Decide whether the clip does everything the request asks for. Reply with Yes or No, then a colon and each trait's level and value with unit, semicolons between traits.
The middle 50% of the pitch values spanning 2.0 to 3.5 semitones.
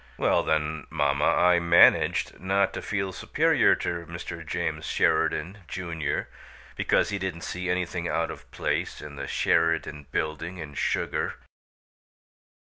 Yes: narrow, 2.6 semitones